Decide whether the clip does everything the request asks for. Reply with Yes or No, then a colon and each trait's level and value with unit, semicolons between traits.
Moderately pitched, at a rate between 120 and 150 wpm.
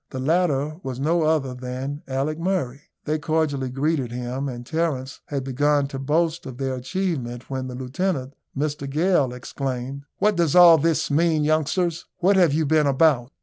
No: medium, 145 Hz; average, 170 wpm